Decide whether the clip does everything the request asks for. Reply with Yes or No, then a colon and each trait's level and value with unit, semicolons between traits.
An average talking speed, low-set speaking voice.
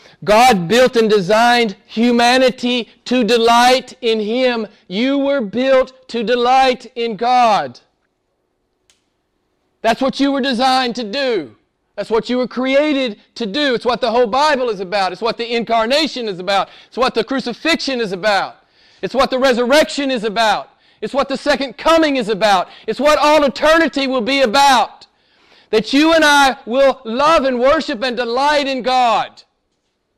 No: average, 160 wpm; very high, 250 Hz